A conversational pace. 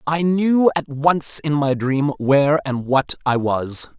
Yes: average, 180 wpm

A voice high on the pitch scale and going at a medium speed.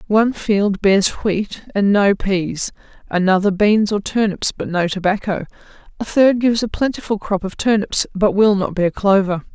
Yes: high, 200 Hz; average, 170 wpm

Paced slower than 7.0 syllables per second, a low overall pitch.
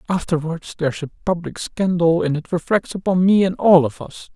No: 5.4 syllables/s; medium, 175 Hz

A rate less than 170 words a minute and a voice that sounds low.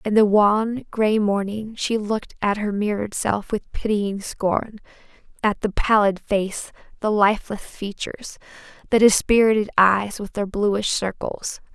No: average, 140 wpm; high, 210 Hz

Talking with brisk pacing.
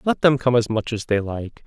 Yes: fast, 290 wpm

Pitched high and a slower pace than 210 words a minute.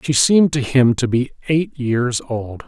No: low, 130 Hz; average, 200 wpm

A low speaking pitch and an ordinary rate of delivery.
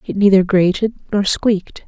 No: high, 195 Hz; average, 160 wpm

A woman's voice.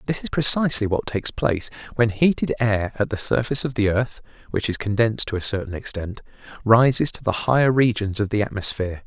No: male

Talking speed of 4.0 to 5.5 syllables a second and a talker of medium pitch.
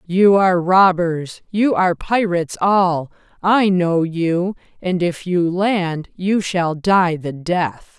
No: 3.3 syllables/s; medium, 180 Hz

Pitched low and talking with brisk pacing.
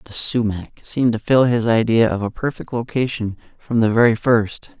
No: low, 115 Hz; average, 190 wpm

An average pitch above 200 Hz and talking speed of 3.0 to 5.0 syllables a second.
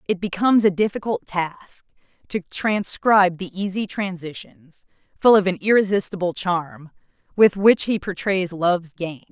No: medium, 185 Hz; 4.6 syllables/s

